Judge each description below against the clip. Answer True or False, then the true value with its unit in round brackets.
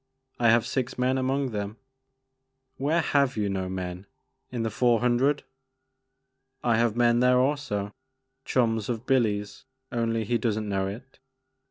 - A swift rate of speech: False (160 wpm)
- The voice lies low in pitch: True (120 Hz)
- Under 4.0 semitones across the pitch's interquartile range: True (3.6 semitones)